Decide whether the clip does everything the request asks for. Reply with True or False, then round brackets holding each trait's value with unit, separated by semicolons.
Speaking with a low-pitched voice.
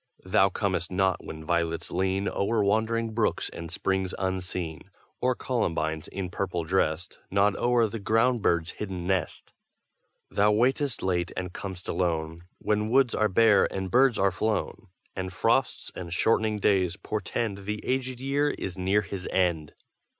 True (95 Hz)